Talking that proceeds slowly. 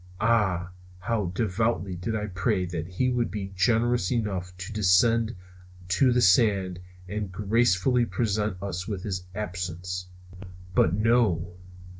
Yes: slow, 130 wpm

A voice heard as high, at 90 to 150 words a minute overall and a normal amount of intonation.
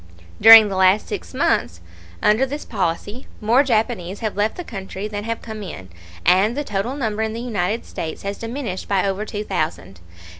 No: high, 210 Hz; average, 185 wpm; average, 3.2 semitones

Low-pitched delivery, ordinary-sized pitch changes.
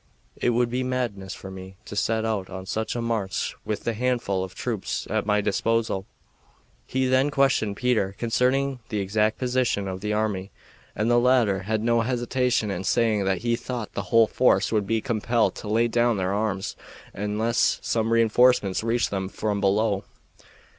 Yes: low, 110 Hz; average, 3.2 semitones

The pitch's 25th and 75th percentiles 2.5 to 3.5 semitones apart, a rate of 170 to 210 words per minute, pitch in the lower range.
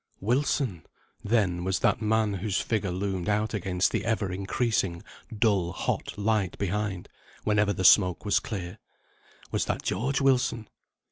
No: average, 2.9 semitones; average, 140 wpm; low, 105 Hz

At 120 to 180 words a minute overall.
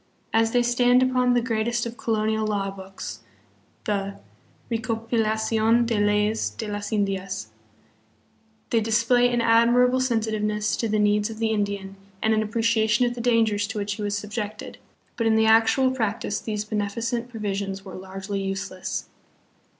Yes: average, 155 wpm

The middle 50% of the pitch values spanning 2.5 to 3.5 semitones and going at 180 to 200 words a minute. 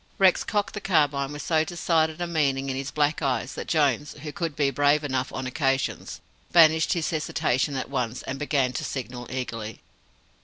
Yes: average, 3.2 semitones; average, 185 wpm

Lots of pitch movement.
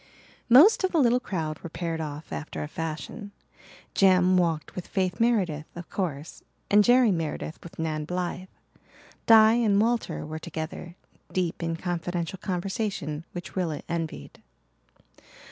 No: average, 4.0 semitones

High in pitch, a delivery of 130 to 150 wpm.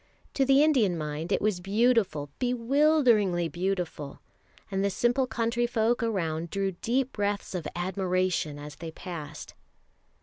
Yes: high, 195 Hz; slow, 135 wpm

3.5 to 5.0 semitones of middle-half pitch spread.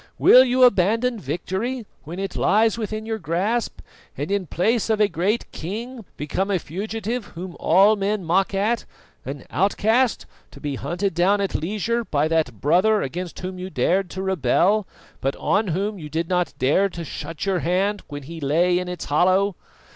Yes: average, 4.1 semitones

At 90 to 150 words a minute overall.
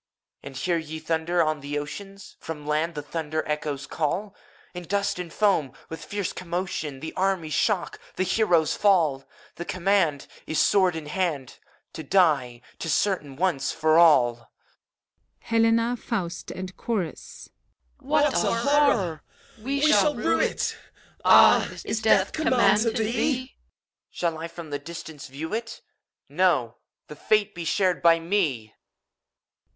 Yes: average, 145 wpm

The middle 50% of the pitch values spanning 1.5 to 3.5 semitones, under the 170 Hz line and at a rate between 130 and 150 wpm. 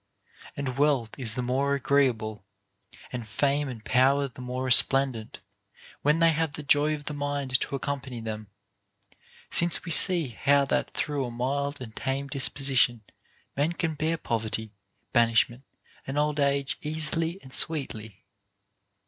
Yes: average, 3.0 semitones; medium, 140 Hz; average, 145 wpm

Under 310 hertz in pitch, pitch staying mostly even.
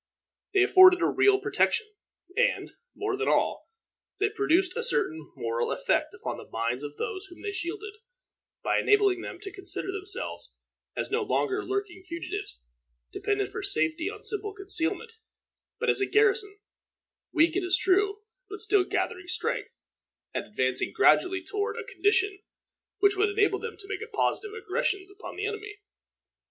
No: very high, 395 Hz; narrow, 2.1 semitones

